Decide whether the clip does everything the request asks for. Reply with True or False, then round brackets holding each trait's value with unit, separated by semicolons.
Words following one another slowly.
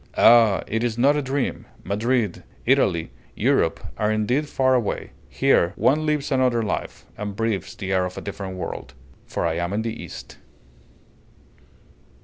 False (155 wpm)